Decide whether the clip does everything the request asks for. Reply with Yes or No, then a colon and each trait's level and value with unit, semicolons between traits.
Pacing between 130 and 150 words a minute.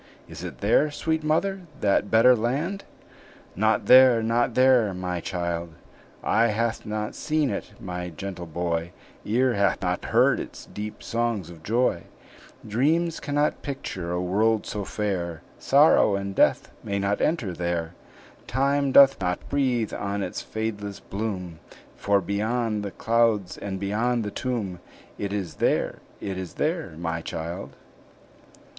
Yes: average, 145 wpm